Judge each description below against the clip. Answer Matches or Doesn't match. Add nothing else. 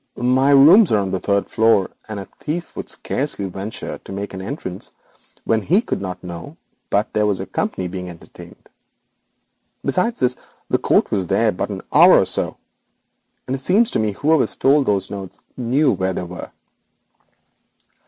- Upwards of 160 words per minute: Matches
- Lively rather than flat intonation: Matches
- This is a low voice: Matches